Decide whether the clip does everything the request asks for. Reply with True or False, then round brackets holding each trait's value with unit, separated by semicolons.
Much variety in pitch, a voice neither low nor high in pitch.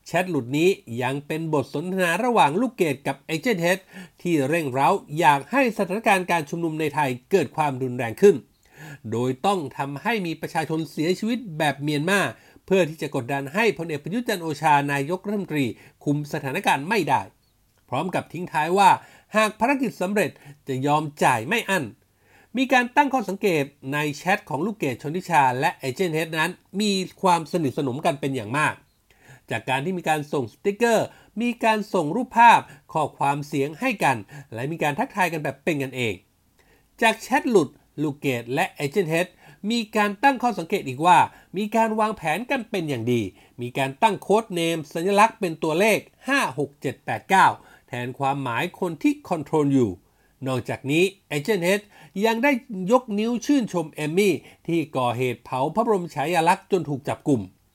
True (6.4 semitones; 165 Hz)